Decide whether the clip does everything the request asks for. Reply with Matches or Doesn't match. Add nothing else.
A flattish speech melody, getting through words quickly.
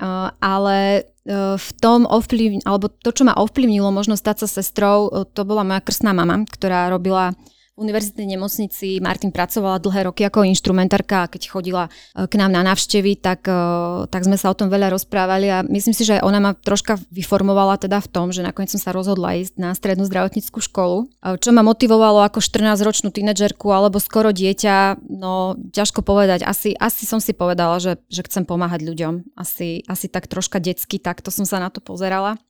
Matches